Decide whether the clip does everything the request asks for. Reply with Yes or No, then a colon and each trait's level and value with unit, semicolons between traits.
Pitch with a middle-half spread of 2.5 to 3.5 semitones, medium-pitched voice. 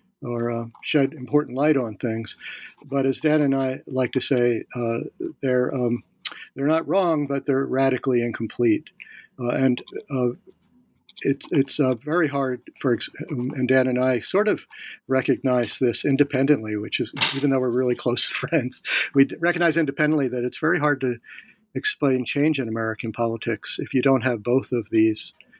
No: average, 2.8 semitones; low, 130 Hz